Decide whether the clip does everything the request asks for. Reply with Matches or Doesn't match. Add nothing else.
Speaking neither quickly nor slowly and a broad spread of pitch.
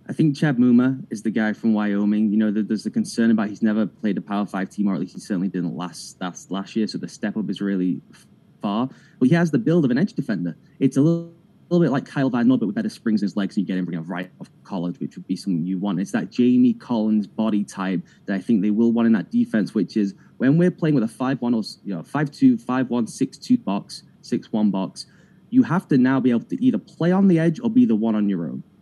Doesn't match